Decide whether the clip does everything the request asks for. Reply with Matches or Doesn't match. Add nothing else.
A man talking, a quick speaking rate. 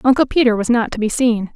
Doesn't match